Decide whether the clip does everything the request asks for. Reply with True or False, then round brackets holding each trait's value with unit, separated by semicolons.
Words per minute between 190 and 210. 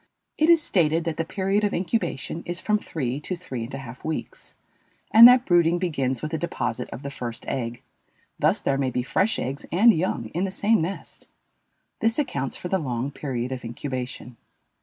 True (195 wpm)